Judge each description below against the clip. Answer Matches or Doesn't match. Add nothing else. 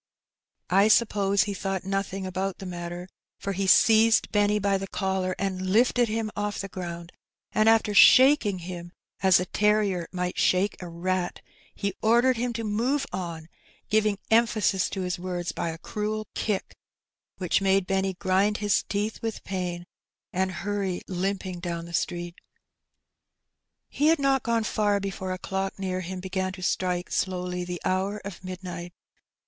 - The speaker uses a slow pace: Doesn't match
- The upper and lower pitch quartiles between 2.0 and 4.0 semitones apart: Matches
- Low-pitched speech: Doesn't match